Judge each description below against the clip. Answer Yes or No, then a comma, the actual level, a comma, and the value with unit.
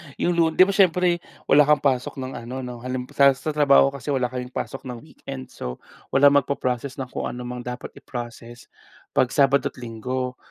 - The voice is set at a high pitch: No, low, 130 Hz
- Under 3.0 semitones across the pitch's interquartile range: Yes, narrow, 2.4 semitones